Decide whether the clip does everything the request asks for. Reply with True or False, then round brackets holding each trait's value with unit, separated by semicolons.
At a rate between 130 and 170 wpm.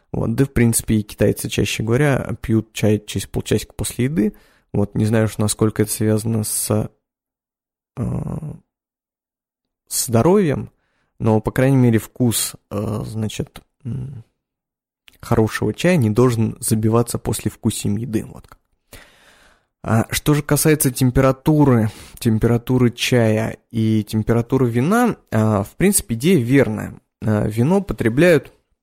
False (120 wpm)